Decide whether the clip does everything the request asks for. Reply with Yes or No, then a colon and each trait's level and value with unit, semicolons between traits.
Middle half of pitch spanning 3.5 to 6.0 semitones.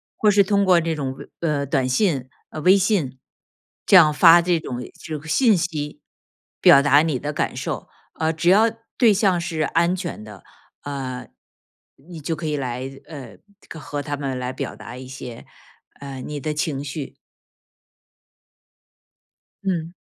Yes: average, 4.1 semitones